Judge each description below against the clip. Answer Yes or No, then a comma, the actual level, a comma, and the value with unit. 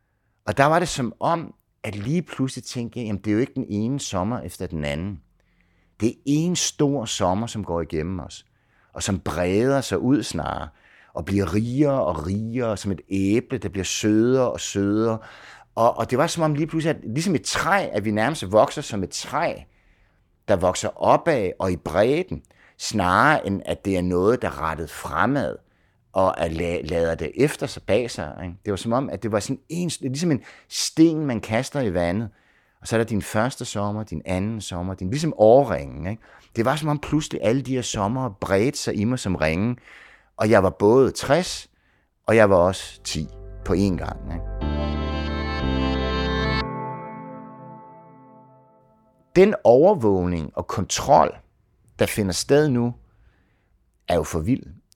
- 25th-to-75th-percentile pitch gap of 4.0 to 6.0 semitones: Yes, wide, 5.6 semitones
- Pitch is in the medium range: No, low, 105 Hz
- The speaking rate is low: No, average, 180 wpm